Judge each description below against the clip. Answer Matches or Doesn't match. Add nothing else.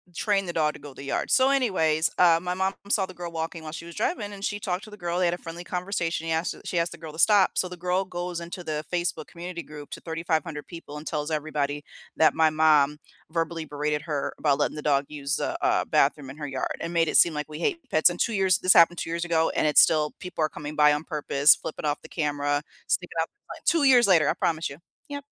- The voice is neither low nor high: Matches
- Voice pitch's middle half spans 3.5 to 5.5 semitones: Doesn't match